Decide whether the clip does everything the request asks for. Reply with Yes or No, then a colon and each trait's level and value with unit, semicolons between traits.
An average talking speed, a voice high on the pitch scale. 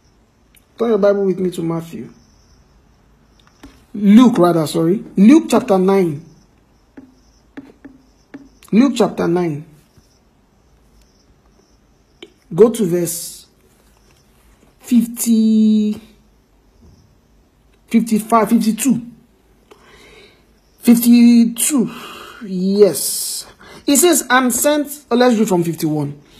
No: slow, 75 wpm; high, 215 Hz